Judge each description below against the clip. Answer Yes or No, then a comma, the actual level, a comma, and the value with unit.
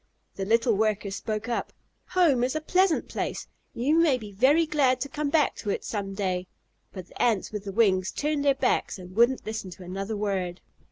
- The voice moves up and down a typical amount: No, wide, 6.2 semitones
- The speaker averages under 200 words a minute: No, fast, 205 wpm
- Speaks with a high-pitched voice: Yes, high, 220 Hz